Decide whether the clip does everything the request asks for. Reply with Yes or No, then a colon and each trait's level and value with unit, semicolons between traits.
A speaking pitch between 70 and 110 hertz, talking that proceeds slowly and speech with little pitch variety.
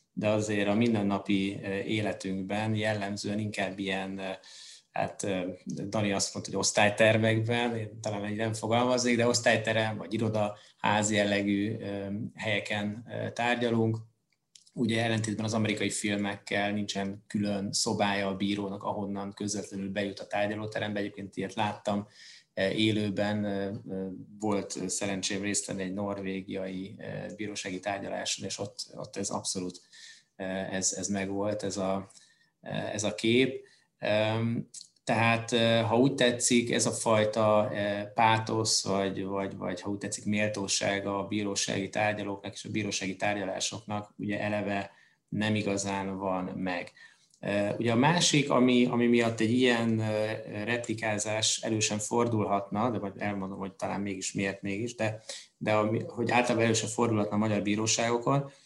No: low, 105 Hz; average, 125 wpm; narrow, 2.1 semitones